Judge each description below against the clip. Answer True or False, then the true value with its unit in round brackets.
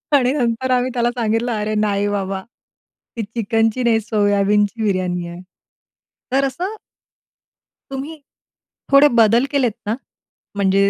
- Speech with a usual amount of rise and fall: True (3.6 semitones)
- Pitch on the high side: True (225 Hz)